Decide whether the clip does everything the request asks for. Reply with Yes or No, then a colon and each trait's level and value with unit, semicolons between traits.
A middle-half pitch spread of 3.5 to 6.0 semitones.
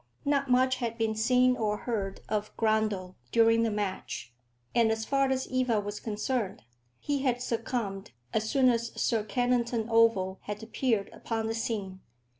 No: average, 2.9 semitones